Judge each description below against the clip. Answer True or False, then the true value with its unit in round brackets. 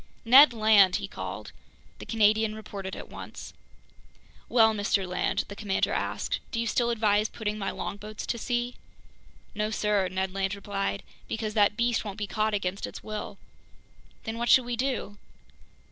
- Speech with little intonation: True (2.0 semitones)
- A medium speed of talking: True (160 wpm)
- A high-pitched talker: True (215 Hz)